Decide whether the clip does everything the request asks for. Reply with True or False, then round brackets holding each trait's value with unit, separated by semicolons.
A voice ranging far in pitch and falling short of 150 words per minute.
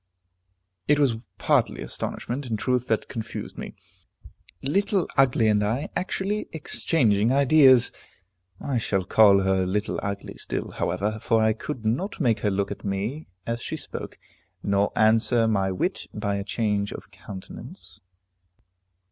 False (4.4 semitones; 140 wpm)